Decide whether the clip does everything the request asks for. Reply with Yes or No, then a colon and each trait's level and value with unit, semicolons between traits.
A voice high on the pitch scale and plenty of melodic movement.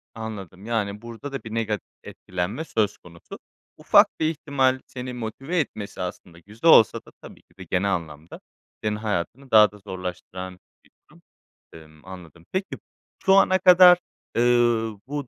No: low, 110 Hz; wide, 6.2 semitones